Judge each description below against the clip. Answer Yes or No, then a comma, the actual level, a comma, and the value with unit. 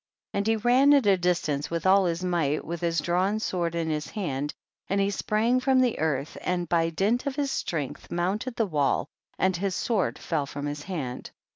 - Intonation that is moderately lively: Yes, average, 5.0 semitones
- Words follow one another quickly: Yes, fast, 210 wpm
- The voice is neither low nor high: Yes, medium, 180 Hz